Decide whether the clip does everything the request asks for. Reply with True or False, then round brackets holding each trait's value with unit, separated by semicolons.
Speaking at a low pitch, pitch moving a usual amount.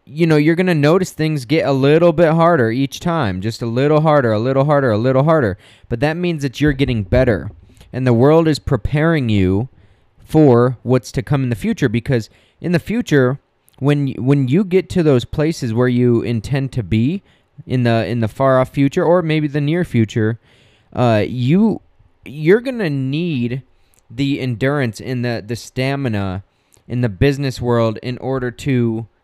True (130 Hz; 4.2 semitones)